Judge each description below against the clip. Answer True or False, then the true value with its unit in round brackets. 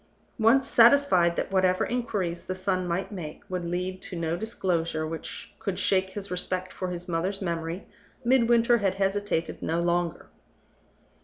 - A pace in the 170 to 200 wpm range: False (150 wpm)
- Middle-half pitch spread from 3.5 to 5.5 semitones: False (2.9 semitones)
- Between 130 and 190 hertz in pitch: True (185 Hz)